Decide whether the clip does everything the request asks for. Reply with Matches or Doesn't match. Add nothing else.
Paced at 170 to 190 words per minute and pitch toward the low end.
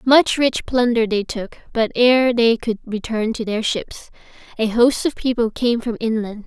Doesn't match